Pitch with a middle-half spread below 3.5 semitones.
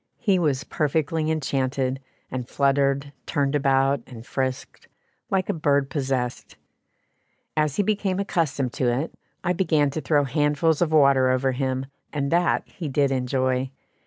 Yes: average, 2.9 semitones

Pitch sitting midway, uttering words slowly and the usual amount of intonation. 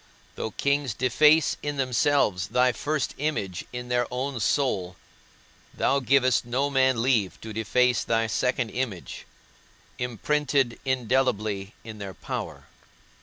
No: low, 125 Hz; slow, 120 wpm; average, 3.5 semitones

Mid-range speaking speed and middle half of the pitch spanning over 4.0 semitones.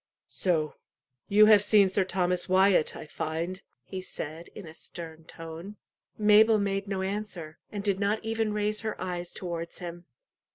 No: average, 160 wpm; average, 3.5 semitones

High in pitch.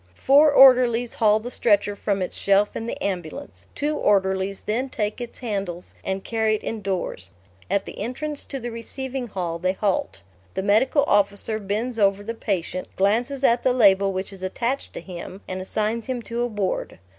Yes: high, 210 Hz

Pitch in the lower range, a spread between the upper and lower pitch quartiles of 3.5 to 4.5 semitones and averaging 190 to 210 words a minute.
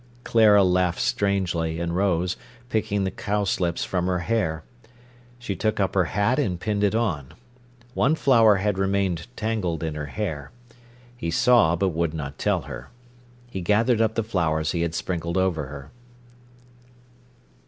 No: very low, 95 Hz; average, 3.8 semitones; average, 155 wpm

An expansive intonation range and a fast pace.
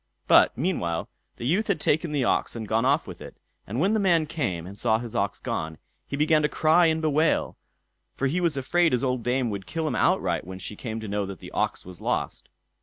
Yes: wide, 7.5 semitones; fast, 235 wpm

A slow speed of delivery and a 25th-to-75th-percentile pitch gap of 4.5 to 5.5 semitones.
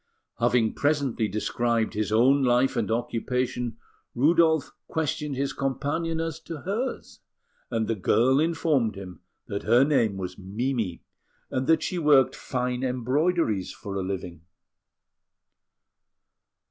Yes: slow, 120 wpm; average, 5.1 semitones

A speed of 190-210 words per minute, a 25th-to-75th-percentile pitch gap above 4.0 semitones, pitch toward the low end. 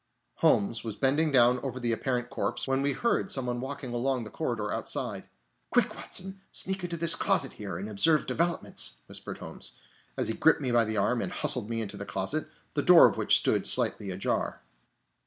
Yes: average, 195 wpm; average, 5.1 semitones; low, 125 Hz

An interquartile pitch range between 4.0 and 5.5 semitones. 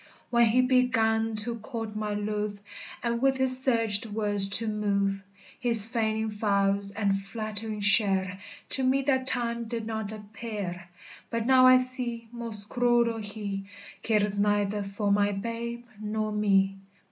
No: narrow, 2.4 semitones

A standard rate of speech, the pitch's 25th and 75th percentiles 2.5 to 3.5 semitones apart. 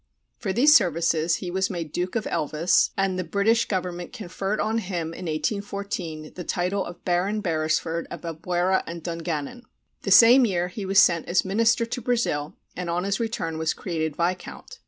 Yes: average, 175 wpm; average, 3.2 semitones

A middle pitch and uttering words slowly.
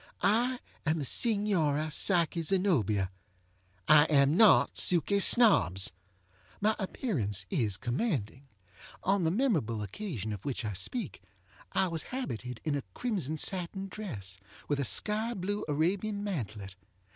Yes: medium, 160 Hz; slow, 130 wpm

